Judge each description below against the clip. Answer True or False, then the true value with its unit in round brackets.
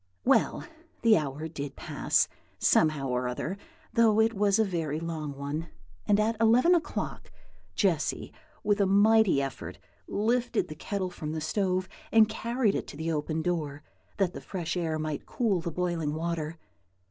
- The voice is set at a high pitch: False (175 Hz)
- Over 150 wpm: True (160 wpm)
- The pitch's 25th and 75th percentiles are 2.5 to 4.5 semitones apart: False (5.4 semitones)